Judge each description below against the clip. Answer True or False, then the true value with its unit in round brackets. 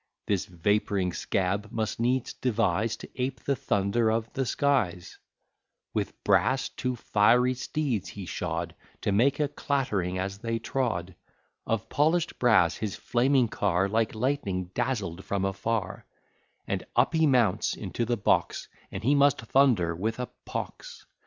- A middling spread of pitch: True (4.9 semitones)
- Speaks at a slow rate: False (145 wpm)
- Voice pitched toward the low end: True (115 Hz)